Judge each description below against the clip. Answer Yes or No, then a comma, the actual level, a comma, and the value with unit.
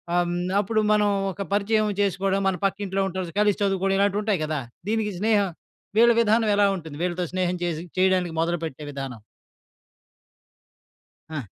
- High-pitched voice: Yes, high, 195 Hz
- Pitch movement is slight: No, average, 3.0 semitones